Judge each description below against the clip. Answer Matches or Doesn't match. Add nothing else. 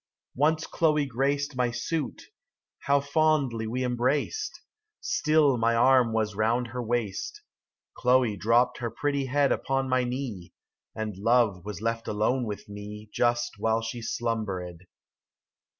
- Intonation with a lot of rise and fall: Doesn't match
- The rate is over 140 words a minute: Doesn't match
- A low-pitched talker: Matches